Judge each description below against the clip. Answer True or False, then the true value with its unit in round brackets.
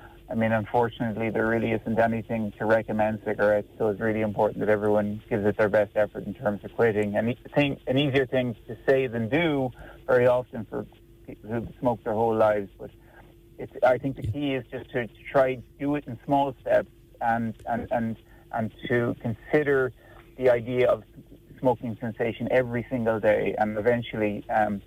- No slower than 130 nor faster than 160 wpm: False (185 wpm)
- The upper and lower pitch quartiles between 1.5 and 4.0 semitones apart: True (2.8 semitones)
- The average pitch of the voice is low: True (115 Hz)